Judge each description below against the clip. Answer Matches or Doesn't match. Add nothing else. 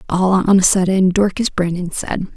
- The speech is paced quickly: Doesn't match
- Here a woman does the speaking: Matches